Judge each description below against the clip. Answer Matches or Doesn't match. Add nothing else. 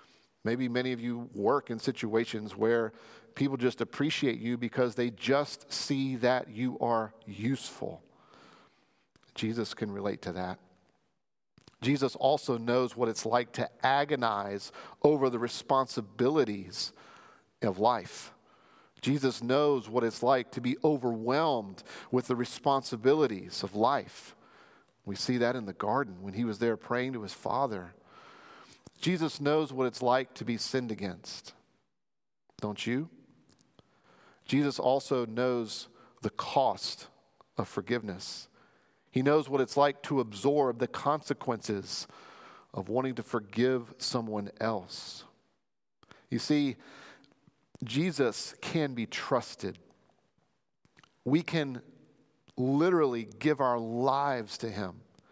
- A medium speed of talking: Doesn't match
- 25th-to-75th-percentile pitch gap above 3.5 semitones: Doesn't match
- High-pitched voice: Doesn't match